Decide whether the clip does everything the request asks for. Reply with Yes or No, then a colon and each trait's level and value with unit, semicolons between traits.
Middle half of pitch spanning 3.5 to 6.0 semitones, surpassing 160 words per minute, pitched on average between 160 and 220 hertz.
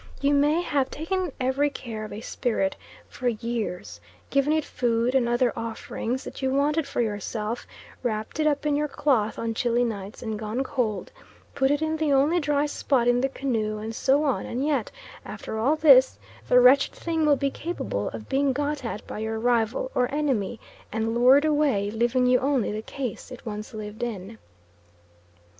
No: average, 4.3 semitones; average, 185 wpm; very high, 250 Hz